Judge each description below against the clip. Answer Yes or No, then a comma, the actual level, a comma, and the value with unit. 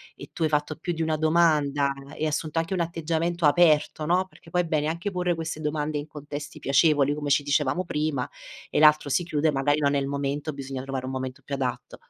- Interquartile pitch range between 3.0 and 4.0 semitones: No, narrow, 2.4 semitones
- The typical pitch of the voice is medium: Yes, medium, 150 Hz